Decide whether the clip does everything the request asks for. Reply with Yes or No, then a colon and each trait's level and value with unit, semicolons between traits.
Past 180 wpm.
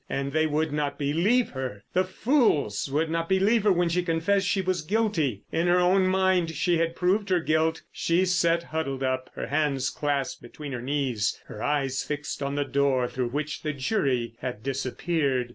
Yes: average, 190 wpm